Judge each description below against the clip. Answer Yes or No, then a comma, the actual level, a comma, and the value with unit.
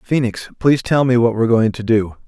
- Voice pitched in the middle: No, low, 115 Hz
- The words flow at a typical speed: No, fast, 240 wpm